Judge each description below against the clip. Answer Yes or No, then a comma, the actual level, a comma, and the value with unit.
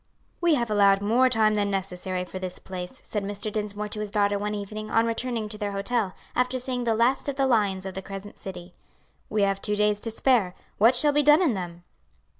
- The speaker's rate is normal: No, fast, 225 wpm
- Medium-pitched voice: No, high, 210 Hz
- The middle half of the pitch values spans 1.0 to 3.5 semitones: Yes, average, 3.2 semitones